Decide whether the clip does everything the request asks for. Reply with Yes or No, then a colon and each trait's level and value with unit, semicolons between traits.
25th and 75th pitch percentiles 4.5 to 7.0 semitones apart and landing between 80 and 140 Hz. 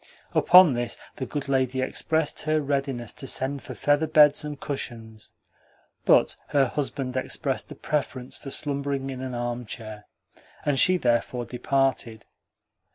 No: average, 3.0 semitones; low, 135 Hz